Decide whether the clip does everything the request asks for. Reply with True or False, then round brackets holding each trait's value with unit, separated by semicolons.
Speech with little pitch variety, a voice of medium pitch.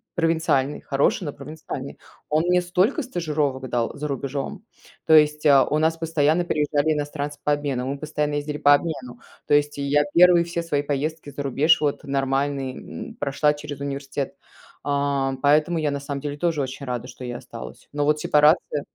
True (1.9 semitones; 145 Hz)